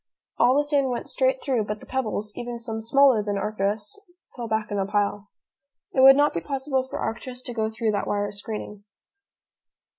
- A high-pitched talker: Yes, high, 225 Hz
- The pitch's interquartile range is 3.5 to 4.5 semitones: Yes, average, 4.2 semitones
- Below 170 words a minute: No, average, 190 wpm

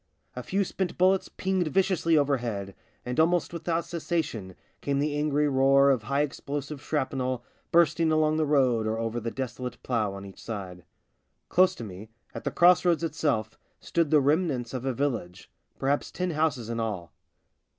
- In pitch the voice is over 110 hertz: Yes, medium, 140 Hz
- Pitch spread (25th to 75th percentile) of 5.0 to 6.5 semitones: Yes, wide, 5.5 semitones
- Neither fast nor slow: Yes, average, 170 wpm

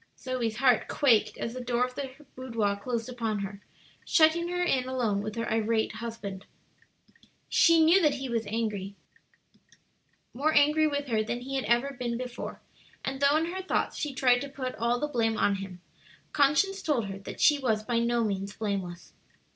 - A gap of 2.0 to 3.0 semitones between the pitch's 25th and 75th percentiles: No, average, 4.3 semitones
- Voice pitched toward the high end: Yes, high, 245 Hz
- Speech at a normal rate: Yes, average, 185 wpm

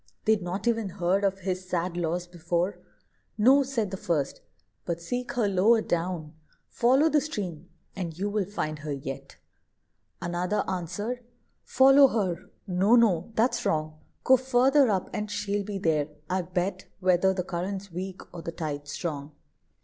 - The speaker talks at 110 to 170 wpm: Yes, average, 155 wpm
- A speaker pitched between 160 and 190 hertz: Yes, medium, 185 Hz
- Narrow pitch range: No, average, 4.0 semitones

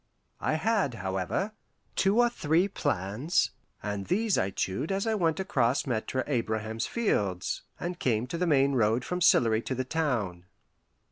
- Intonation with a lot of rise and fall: Yes, wide, 8.5 semitones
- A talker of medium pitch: No, low, 130 Hz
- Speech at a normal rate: Yes, average, 155 wpm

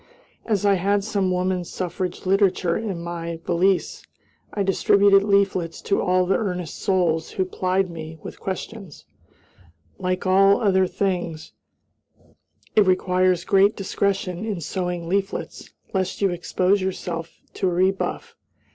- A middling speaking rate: No, slow, 130 wpm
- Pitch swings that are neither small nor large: No, narrow, 1.8 semitones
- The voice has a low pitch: No, medium, 185 Hz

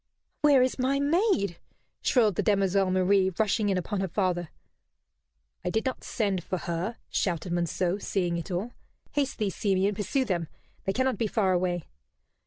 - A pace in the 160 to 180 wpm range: Yes, average, 165 wpm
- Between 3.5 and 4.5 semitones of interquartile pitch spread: Yes, average, 3.9 semitones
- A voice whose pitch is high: Yes, high, 195 Hz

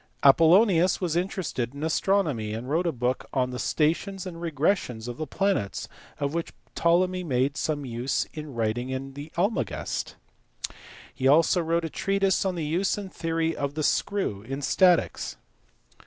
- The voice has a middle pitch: Yes, medium, 160 Hz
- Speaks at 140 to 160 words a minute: Yes, average, 155 wpm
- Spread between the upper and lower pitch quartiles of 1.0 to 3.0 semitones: No, wide, 5.4 semitones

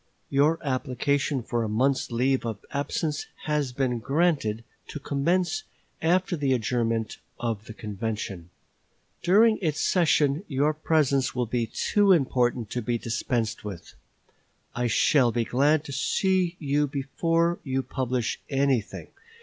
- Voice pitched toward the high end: No, low, 135 Hz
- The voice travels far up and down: No, average, 4.4 semitones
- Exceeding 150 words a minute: No, slow, 135 wpm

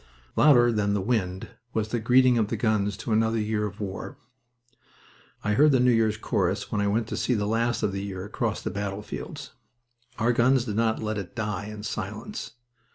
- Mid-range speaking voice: No, low, 110 Hz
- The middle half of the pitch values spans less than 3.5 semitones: Yes, narrow, 2.4 semitones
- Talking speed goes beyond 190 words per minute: Yes, average, 200 wpm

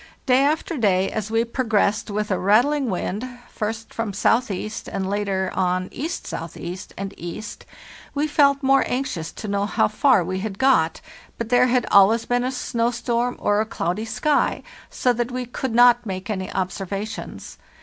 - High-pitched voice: Yes, high, 220 Hz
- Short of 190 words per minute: Yes, average, 170 wpm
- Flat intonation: No, average, 4.1 semitones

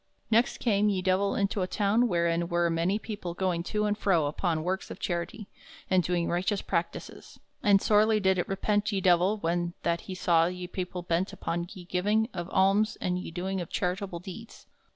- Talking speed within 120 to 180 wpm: No, average, 195 wpm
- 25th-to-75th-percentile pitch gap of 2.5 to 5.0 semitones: Yes, average, 2.8 semitones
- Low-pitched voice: No, medium, 185 Hz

